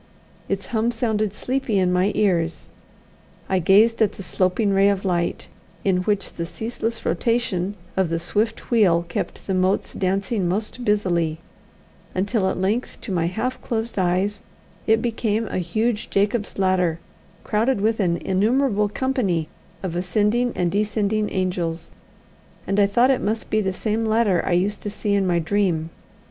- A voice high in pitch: Yes, high, 200 Hz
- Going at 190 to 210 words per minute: No, average, 160 wpm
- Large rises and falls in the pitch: No, average, 3.3 semitones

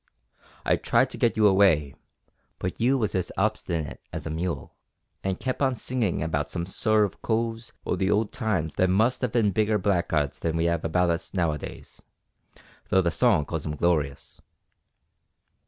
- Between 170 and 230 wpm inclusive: Yes, average, 180 wpm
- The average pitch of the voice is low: Yes, very low, 95 Hz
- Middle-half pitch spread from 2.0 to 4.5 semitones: No, average, 4.9 semitones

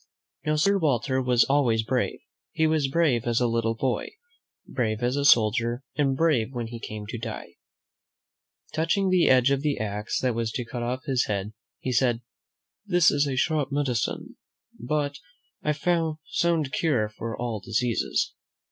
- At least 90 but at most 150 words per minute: No, average, 165 wpm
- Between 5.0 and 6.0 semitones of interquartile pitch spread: No, average, 4.5 semitones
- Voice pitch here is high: No, low, 130 Hz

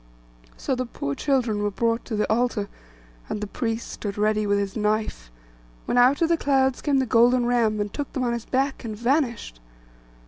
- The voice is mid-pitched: No, high, 235 Hz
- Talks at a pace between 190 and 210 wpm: Yes, average, 200 wpm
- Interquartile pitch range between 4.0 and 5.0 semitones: No, average, 3.4 semitones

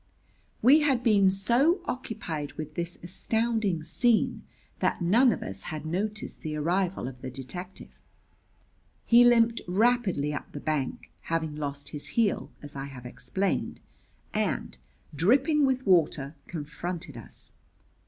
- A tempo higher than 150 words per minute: No, slow, 135 wpm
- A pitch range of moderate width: No, wide, 7.6 semitones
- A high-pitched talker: No, medium, 180 Hz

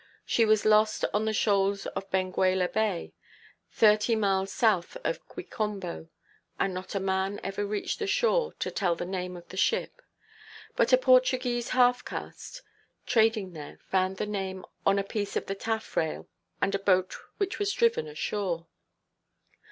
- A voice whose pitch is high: Yes, high, 205 Hz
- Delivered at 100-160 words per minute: Yes, average, 155 wpm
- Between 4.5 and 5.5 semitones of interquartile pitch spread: No, average, 3.3 semitones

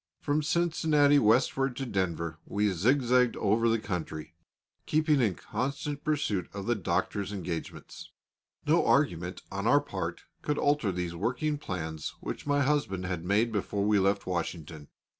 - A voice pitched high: No, low, 105 Hz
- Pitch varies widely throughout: Yes, wide, 7.7 semitones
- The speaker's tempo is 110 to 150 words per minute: Yes, average, 145 wpm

